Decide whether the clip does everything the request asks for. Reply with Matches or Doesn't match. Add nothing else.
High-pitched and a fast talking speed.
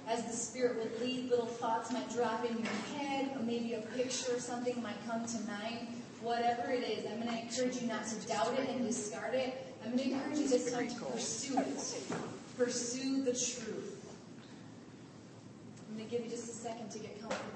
Matches